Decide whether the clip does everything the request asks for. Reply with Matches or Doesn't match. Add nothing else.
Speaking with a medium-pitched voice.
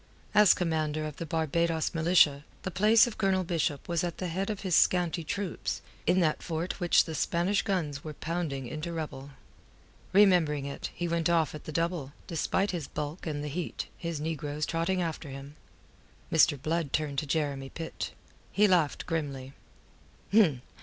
Matches